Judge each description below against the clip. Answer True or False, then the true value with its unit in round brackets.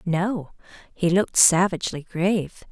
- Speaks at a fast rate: False (110 wpm)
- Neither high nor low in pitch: True (180 Hz)